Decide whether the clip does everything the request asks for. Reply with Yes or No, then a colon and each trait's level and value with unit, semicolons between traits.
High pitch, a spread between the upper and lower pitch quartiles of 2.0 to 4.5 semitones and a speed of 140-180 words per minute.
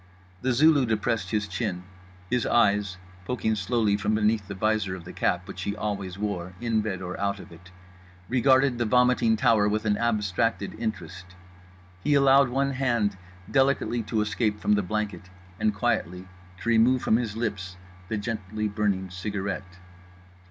No: low, 105 Hz; average, 3.1 semitones; average, 160 wpm